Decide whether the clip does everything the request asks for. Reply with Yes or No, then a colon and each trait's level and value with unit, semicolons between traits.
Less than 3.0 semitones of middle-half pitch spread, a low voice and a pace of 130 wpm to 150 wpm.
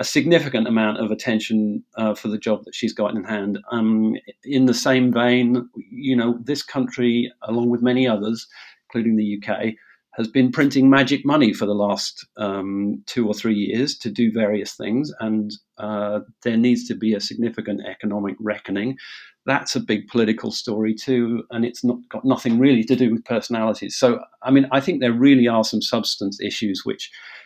No: narrow, 2.6 semitones; low, 115 Hz; average, 185 wpm